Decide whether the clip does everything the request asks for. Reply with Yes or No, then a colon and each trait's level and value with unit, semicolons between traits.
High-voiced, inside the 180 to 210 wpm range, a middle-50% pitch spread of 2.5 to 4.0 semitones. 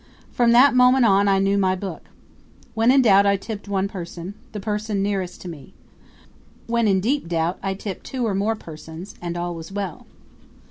Yes: high, 200 Hz; average, 190 wpm; average, 3.4 semitones